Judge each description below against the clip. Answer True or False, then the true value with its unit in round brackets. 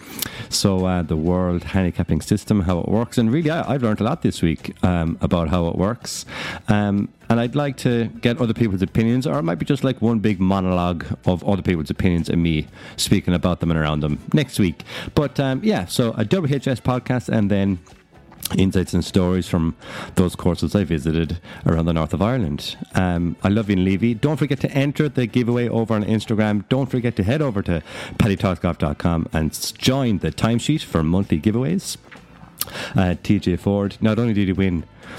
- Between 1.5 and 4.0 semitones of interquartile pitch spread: False (5.1 semitones)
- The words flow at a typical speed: True (195 wpm)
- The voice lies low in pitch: True (100 Hz)